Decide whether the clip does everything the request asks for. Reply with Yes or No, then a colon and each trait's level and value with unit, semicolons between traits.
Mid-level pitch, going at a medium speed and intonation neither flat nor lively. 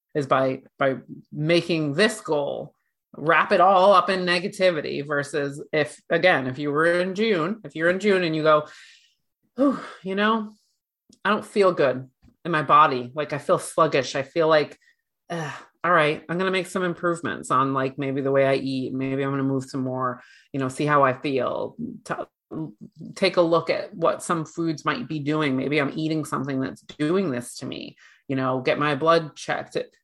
Yes: medium, 155 Hz; average, 195 wpm; average, 4.7 semitones